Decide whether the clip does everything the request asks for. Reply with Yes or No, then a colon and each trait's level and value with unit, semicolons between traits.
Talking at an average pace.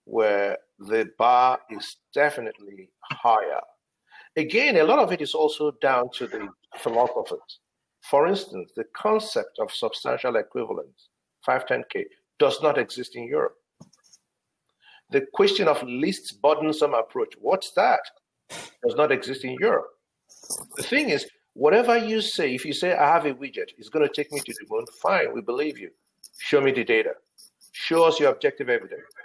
Yes: average, 160 wpm